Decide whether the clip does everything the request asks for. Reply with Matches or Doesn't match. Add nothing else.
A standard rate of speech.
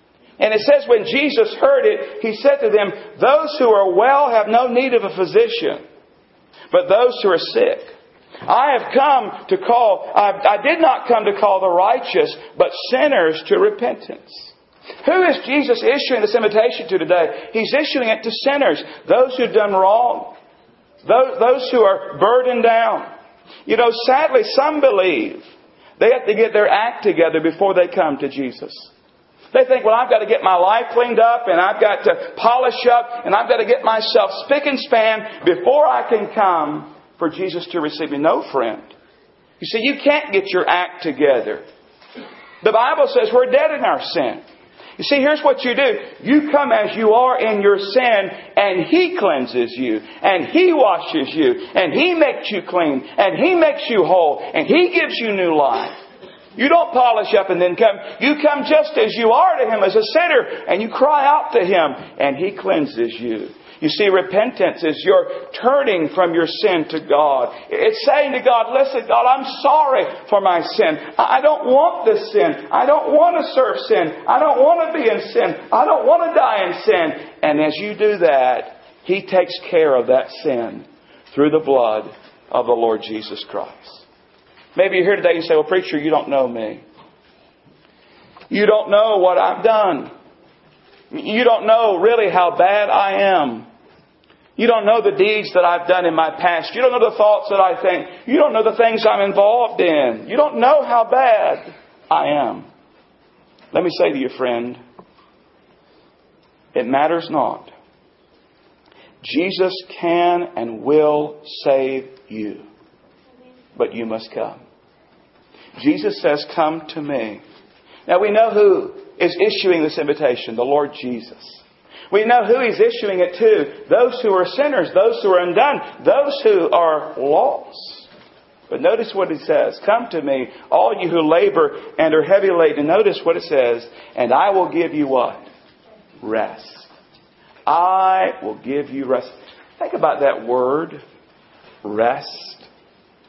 Matches